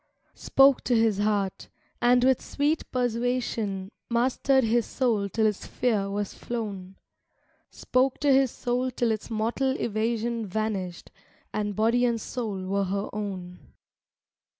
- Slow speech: Yes, slow, 130 wpm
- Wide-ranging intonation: No, average, 3.4 semitones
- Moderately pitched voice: No, high, 225 Hz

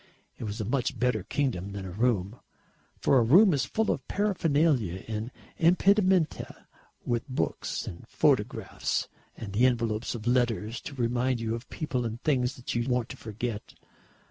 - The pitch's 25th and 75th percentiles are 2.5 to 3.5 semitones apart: No, average, 4.0 semitones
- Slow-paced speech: No, average, 165 wpm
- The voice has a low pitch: Yes, low, 120 Hz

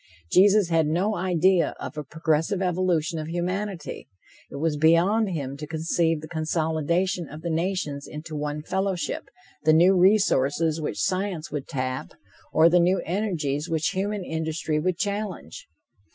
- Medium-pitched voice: Yes, medium, 165 Hz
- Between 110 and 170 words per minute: Yes, average, 150 wpm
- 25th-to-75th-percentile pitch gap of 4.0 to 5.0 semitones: No, average, 3.2 semitones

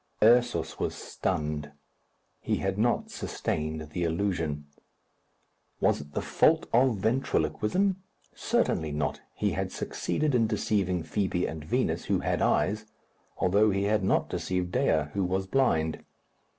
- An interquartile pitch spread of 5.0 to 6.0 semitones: Yes, wide, 5.4 semitones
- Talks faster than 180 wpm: No, slow, 135 wpm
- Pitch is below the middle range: Yes, very low, 95 Hz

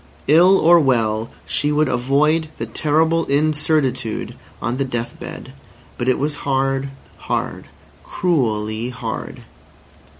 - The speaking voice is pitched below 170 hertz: Yes, low, 135 Hz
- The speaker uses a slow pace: Yes, slow, 120 wpm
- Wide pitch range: No, average, 4.1 semitones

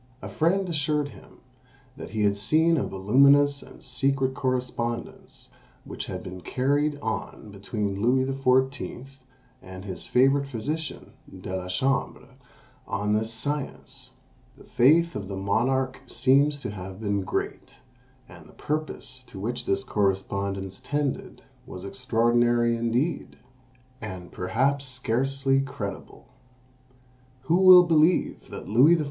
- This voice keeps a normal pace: No, slow, 130 wpm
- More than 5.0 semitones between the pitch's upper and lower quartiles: Yes, wide, 5.4 semitones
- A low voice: Yes, low, 125 Hz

